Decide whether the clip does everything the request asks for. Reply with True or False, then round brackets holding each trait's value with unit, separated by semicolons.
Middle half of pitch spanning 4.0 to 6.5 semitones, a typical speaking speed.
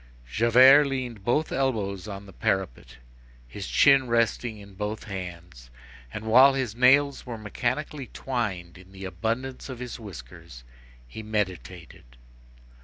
False (5.1 semitones; 130 wpm)